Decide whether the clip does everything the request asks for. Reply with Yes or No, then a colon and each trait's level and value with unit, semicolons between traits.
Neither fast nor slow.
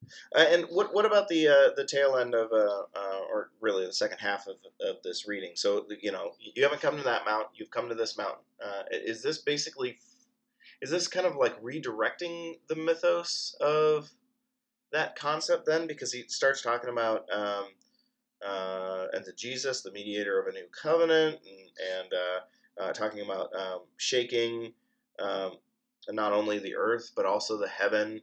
Yes: average, 185 wpm